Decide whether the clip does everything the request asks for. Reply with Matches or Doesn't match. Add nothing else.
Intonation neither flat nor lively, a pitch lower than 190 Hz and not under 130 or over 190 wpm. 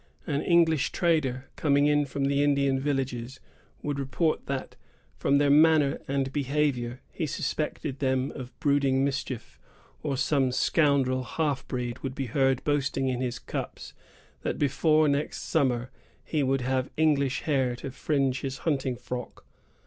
Doesn't match